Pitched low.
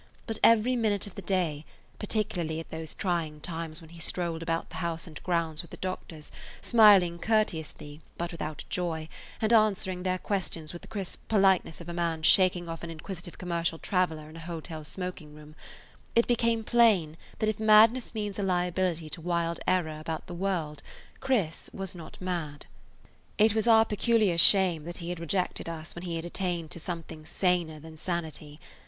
No: medium, 175 Hz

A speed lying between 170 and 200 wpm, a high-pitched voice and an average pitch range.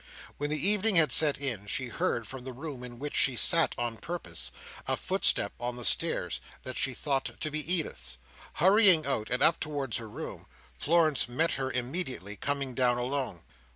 No: average, 185 wpm; low, 135 Hz; average, 4.1 semitones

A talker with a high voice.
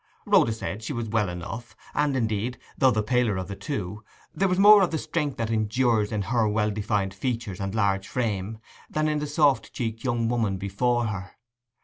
No: low, 115 Hz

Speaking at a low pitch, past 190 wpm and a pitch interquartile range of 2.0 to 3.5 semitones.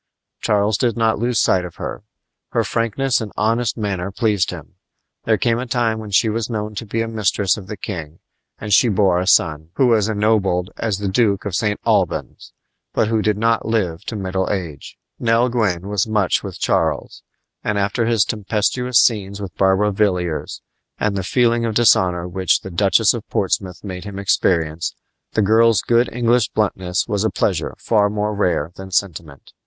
No: low, 105 Hz; average, 185 wpm; average, 3.2 semitones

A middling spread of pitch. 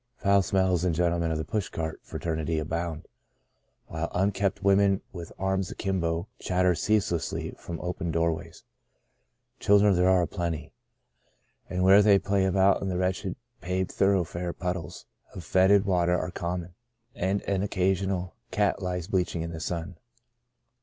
No: narrow, 2.2 semitones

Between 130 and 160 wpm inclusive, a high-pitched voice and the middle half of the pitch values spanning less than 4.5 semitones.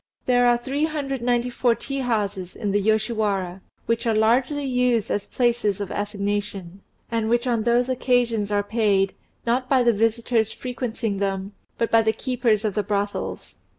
Yes: average, 155 wpm; high, 225 Hz; average, 3.1 semitones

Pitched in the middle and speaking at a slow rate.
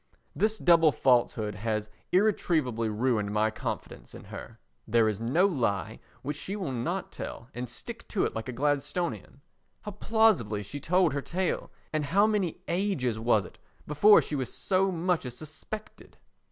No: medium, 145 Hz; average, 160 wpm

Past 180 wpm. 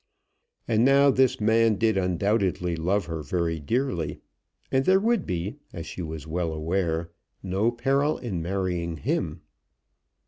No: average, 140 wpm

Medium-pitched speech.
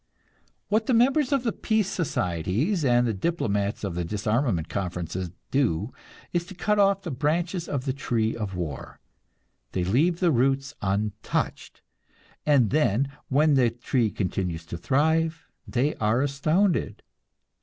No: low, 130 Hz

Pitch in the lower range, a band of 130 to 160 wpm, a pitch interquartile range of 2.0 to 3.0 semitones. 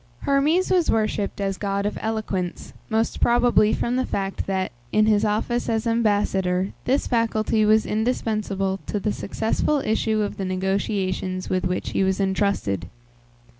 No: high, 210 Hz; average, 150 wpm; narrow, 2.6 semitones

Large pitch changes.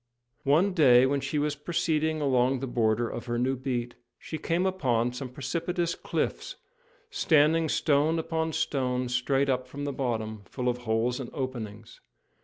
No: average, 3.9 semitones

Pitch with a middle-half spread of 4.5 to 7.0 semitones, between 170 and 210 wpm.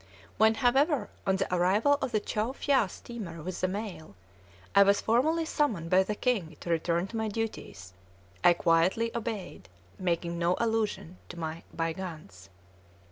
No: average, 5.0 semitones; average, 155 wpm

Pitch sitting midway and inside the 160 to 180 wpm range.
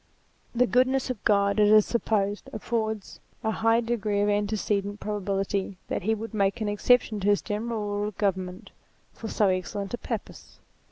No: high, 210 Hz; average, 175 wpm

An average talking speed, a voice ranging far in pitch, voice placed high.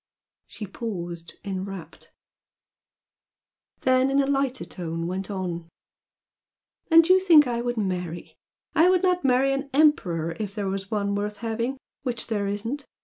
Yes: average, 145 wpm; wide, 6.5 semitones; high, 215 Hz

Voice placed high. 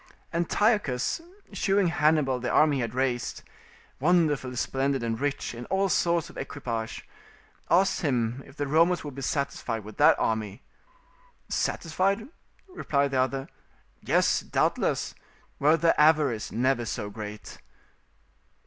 No: medium, 140 Hz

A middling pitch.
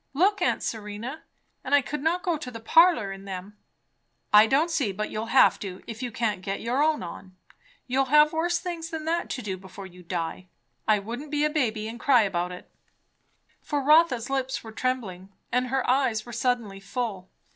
No: high, 240 Hz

